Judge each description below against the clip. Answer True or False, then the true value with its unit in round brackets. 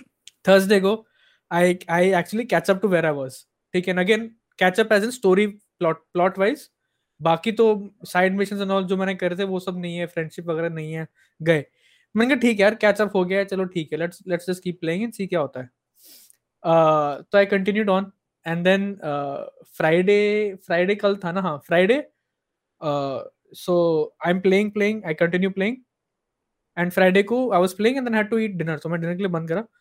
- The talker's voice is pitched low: False (185 Hz)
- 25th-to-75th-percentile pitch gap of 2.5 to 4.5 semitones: True (3.4 semitones)